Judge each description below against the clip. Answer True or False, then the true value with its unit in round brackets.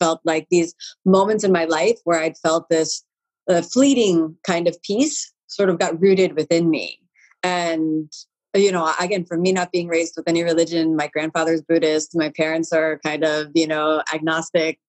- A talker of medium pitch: True (165 Hz)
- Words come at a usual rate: True (180 wpm)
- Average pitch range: False (2.2 semitones)